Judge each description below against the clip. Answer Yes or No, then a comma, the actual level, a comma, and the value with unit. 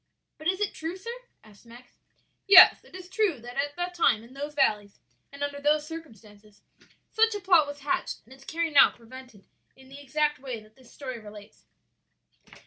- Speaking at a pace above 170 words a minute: Yes, average, 190 wpm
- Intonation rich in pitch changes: Yes, wide, 5.7 semitones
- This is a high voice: Yes, very high, 285 Hz